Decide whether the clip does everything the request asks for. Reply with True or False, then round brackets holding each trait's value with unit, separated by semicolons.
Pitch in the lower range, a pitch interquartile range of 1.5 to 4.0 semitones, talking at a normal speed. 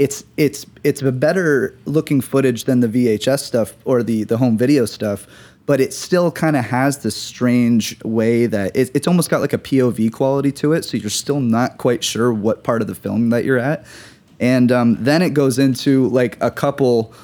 False (125 Hz; 3.3 semitones; 210 wpm)